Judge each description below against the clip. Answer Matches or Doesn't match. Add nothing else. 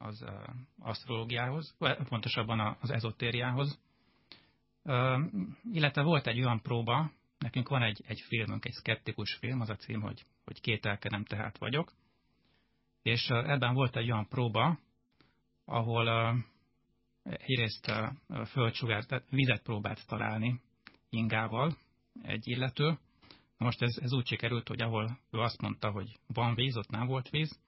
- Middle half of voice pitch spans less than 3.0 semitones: Matches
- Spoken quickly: Doesn't match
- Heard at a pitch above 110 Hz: Matches